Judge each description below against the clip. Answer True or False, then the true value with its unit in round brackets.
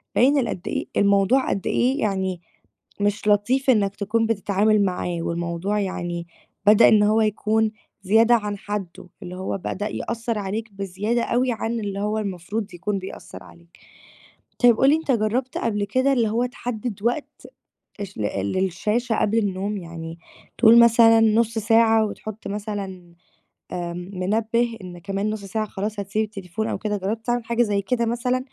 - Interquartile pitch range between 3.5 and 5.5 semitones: False (2.7 semitones)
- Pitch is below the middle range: False (210 Hz)